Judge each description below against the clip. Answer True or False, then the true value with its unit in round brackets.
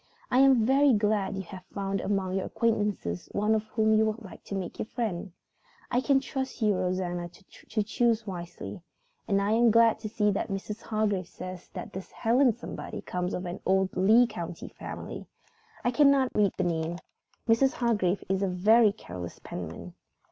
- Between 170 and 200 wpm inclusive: True (175 wpm)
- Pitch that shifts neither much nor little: True (3.7 semitones)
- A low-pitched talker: False (205 Hz)